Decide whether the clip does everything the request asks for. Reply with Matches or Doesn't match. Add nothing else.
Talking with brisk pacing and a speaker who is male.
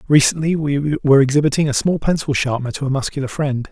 Doesn't match